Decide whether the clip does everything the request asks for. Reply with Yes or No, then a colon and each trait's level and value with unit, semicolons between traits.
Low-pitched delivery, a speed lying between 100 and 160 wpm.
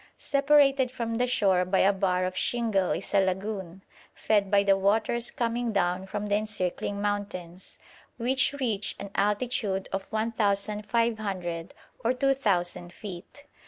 No: high, 205 Hz; slow, 135 wpm